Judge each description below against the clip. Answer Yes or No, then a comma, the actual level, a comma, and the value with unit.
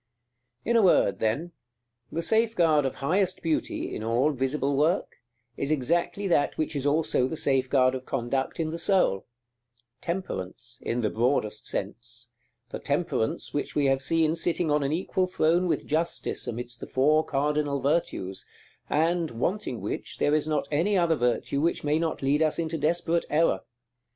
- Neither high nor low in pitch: Yes, medium, 150 Hz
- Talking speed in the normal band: Yes, average, 170 wpm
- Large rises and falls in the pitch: No, average, 4.3 semitones